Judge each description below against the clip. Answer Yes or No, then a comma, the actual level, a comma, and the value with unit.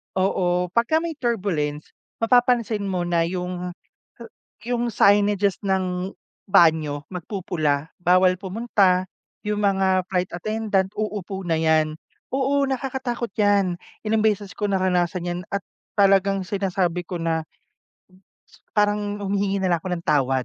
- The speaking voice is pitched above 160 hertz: Yes, high, 190 Hz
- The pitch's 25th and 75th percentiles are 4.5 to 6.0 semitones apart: No, average, 2.7 semitones